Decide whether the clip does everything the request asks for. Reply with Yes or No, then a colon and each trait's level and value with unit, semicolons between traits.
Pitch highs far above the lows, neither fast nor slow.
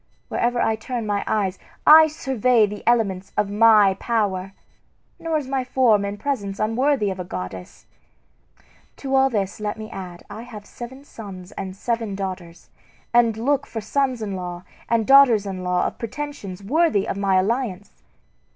No: average, 4.4 semitones; average, 165 wpm